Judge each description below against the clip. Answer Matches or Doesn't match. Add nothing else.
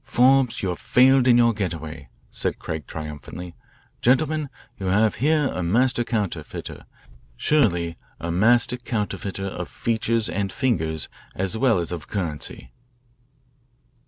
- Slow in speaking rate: Matches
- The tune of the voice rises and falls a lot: Matches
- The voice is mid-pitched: Doesn't match